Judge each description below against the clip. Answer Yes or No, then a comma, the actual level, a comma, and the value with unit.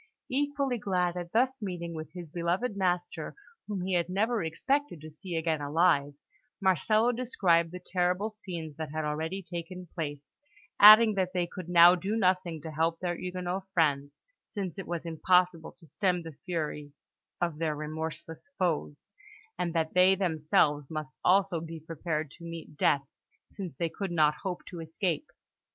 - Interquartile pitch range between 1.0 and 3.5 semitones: Yes, average, 2.9 semitones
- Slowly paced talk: No, average, 165 wpm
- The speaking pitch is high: No, medium, 175 Hz